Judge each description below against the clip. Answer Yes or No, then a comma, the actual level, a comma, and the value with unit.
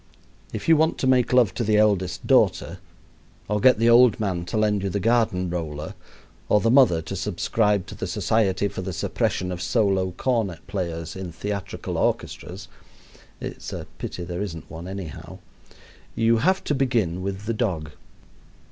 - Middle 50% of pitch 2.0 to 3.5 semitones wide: No, average, 4.1 semitones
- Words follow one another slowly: No, average, 170 wpm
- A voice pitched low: Yes, low, 100 Hz